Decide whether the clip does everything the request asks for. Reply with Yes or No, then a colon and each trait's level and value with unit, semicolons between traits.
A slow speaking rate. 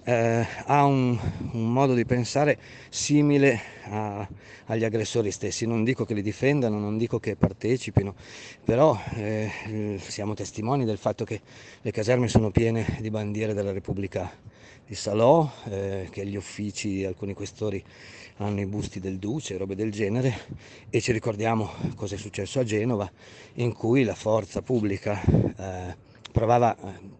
No: average, 150 wpm